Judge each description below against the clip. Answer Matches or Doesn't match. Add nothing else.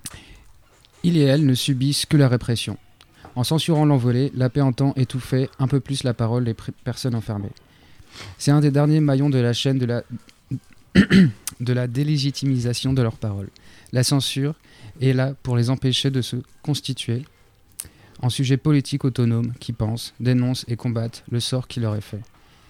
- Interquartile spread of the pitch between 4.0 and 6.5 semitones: Doesn't match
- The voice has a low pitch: Matches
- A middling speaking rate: Matches